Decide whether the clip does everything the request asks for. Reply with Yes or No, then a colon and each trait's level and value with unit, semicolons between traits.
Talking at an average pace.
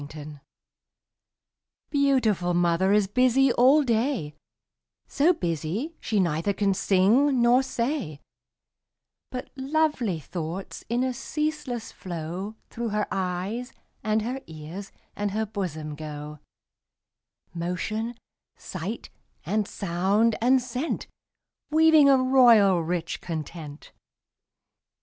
No: slow, 105 wpm